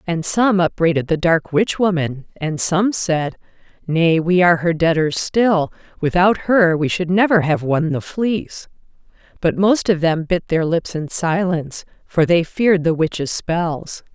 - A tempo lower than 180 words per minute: Yes, average, 170 wpm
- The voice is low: No, medium, 170 Hz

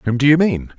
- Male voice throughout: Yes, male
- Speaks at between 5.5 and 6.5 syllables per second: Yes, 5.6 syllables/s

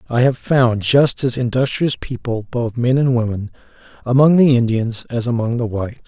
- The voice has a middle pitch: No, low, 120 Hz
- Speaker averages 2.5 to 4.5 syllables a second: No, 5.0 syllables/s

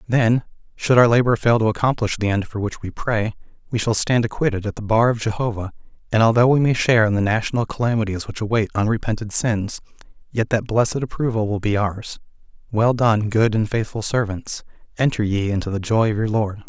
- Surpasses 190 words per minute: Yes, average, 200 wpm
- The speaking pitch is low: Yes, low, 110 Hz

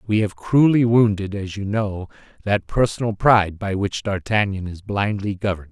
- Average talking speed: Yes, average, 170 wpm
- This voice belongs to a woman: No, male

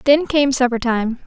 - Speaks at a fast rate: No, average, 190 wpm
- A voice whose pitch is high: Yes, very high, 260 Hz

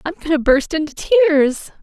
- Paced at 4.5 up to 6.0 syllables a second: No, 4.3 syllables/s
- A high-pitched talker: Yes, very high, 280 Hz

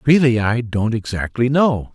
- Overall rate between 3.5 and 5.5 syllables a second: Yes, 4.4 syllables/s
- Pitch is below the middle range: Yes, low, 120 Hz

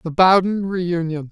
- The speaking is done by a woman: No, male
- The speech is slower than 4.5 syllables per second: Yes, 4.1 syllables/s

